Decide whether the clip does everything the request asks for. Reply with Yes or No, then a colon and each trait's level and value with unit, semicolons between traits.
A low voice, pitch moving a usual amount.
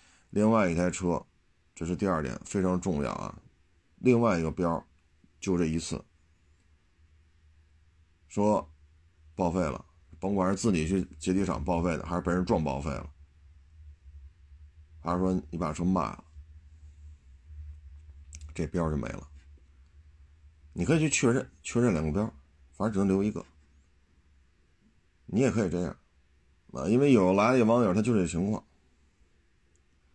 Yes: very low, 80 Hz; average, 3.5 semitones